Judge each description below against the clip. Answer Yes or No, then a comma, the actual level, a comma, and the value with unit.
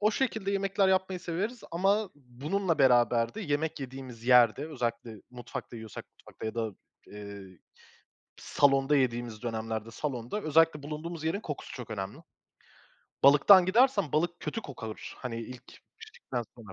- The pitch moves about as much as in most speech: No, wide, 7.7 semitones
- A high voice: No, medium, 140 Hz